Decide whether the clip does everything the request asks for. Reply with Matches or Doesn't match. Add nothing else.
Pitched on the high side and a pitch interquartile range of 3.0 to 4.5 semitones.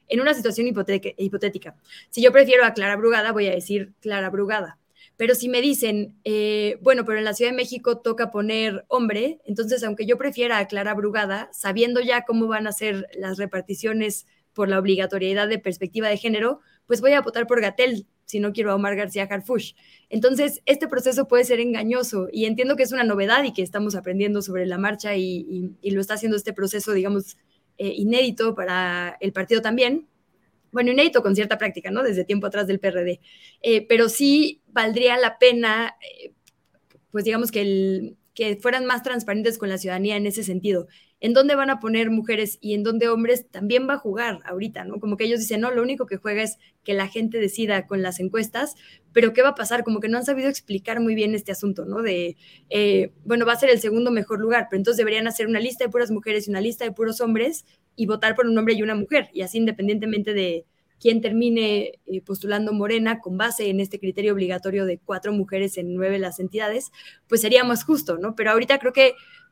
Matches